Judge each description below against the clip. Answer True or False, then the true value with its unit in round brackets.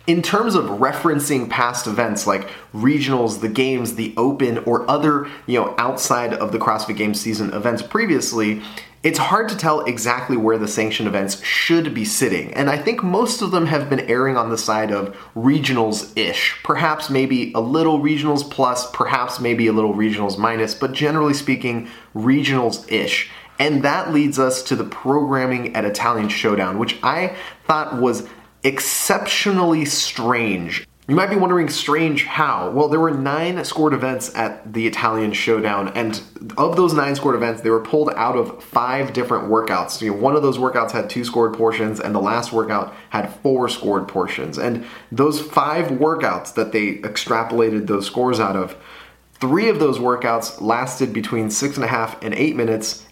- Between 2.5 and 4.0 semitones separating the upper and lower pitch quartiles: False (4.6 semitones)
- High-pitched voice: False (125 Hz)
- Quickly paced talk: False (175 wpm)